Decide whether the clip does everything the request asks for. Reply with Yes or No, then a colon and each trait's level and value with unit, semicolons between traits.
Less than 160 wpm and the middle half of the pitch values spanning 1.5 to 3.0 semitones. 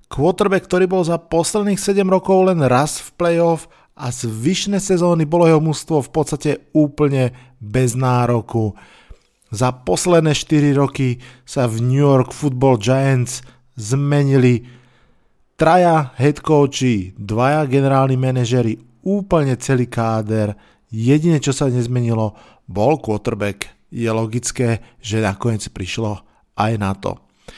No: average, 125 wpm; average, 4.5 semitones